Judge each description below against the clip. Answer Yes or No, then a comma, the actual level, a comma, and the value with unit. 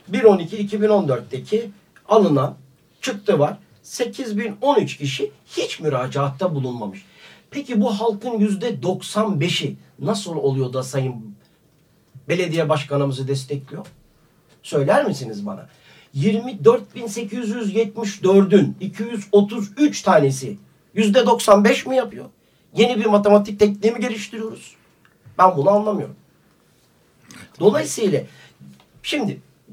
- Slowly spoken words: Yes, slow, 85 wpm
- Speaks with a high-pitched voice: Yes, high, 200 Hz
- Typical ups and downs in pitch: No, wide, 7.4 semitones